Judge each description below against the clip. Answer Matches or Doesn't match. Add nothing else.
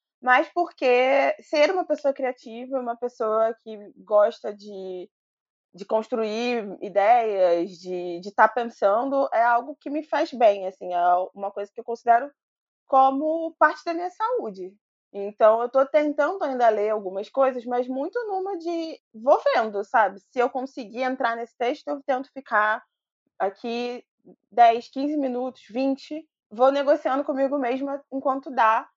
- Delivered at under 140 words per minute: Doesn't match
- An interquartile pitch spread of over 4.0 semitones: Matches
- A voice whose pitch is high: Matches